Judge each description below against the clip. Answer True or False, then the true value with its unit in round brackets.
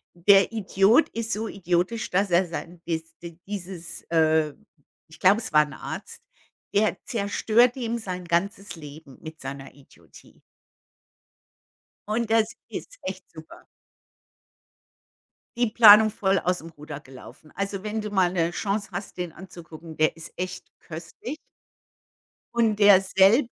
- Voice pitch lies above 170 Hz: True (185 Hz)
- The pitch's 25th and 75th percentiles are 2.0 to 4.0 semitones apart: False (4.4 semitones)